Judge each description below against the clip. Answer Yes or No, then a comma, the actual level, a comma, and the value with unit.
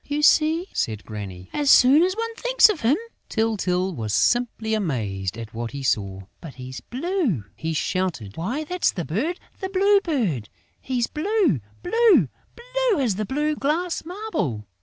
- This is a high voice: Yes, high, 240 Hz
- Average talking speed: Yes, average, 160 wpm